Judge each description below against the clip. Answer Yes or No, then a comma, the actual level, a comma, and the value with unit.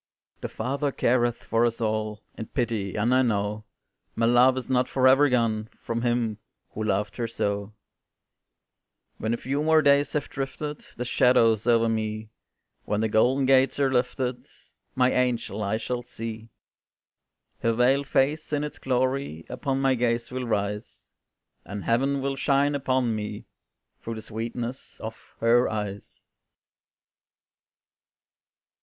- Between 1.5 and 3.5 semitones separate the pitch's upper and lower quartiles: Yes, average, 3.2 semitones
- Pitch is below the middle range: Yes, low, 120 Hz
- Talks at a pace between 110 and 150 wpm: Yes, average, 140 wpm